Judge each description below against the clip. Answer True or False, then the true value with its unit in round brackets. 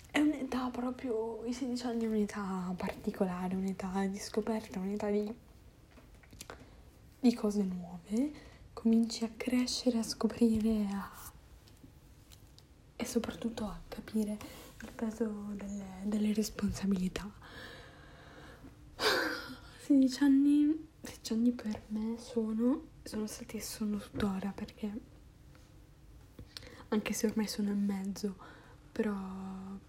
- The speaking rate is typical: False (100 wpm)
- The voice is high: True (220 Hz)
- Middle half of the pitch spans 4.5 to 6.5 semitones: False (3.0 semitones)